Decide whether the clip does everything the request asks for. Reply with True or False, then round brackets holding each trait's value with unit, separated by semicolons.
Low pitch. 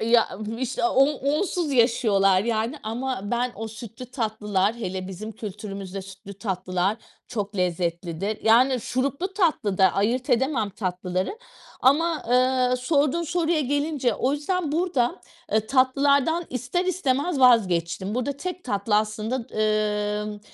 False (240 Hz)